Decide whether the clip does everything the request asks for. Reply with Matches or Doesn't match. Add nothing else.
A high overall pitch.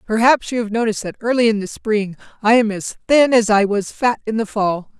Matches